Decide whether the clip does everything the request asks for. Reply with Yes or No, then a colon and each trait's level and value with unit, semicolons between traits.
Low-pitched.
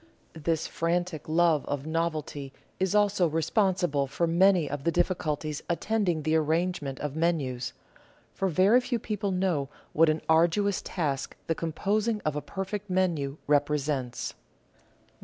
No: medium, 165 Hz